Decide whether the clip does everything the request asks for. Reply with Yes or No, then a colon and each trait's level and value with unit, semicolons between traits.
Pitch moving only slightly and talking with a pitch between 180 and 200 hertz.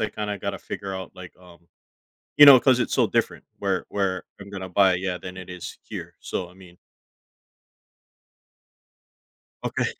No: narrow, 1.9 semitones; very low, 95 Hz